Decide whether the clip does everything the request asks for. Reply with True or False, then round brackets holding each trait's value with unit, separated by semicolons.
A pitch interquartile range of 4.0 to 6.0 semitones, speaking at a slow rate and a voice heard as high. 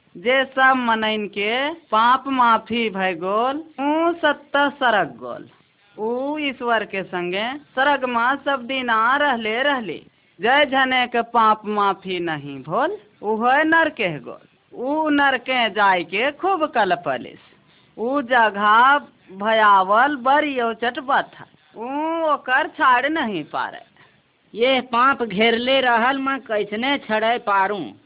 False (4.5 semitones; 125 wpm; 250 Hz)